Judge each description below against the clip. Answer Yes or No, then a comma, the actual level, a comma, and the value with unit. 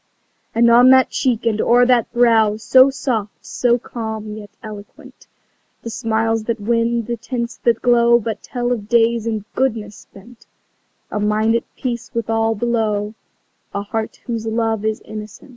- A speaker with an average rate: Yes, average, 160 wpm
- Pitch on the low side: No, high, 225 Hz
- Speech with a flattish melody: Yes, narrow, 1.6 semitones